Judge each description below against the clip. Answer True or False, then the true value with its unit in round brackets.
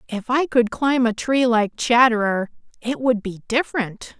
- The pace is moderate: True (170 wpm)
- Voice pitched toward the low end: False (235 Hz)